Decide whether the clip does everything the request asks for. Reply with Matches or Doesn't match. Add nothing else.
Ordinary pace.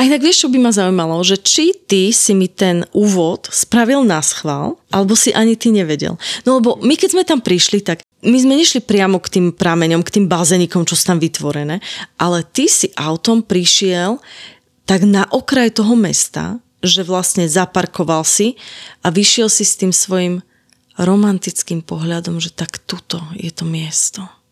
Doesn't match